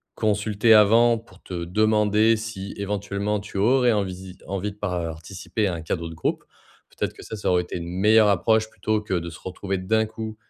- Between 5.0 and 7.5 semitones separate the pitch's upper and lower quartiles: No, average, 2.9 semitones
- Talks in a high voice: No, low, 105 Hz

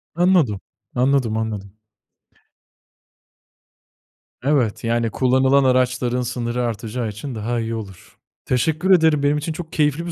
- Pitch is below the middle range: Yes, low, 125 Hz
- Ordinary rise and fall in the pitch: Yes, average, 4.4 semitones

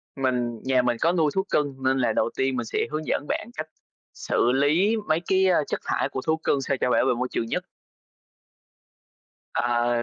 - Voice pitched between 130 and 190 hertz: Yes, low, 135 Hz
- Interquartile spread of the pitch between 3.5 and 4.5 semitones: Yes, average, 4.1 semitones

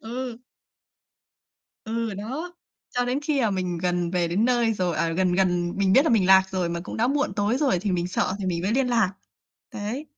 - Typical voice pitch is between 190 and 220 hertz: Yes, high, 200 Hz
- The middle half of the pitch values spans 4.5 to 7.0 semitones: Yes, average, 5.1 semitones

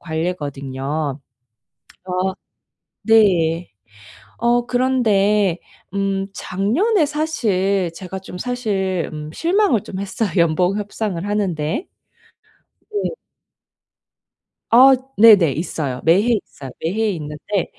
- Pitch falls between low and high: No, high, 195 Hz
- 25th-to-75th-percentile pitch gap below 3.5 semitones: No, average, 5.1 semitones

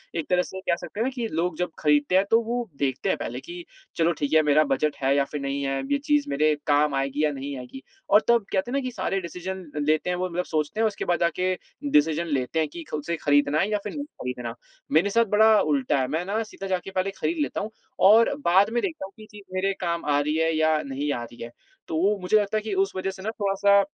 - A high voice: No, medium, 175 Hz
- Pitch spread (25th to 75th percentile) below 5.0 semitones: No, wide, 5.4 semitones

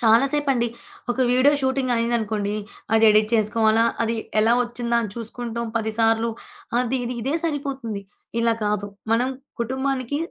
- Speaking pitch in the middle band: No, high, 235 Hz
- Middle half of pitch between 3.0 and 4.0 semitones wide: No, narrow, 2.4 semitones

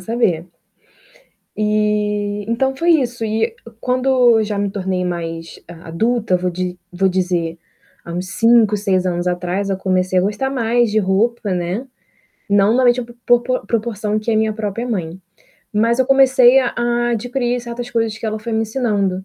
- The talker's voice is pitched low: No, high, 215 Hz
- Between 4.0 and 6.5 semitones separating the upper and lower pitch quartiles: Yes, average, 4.3 semitones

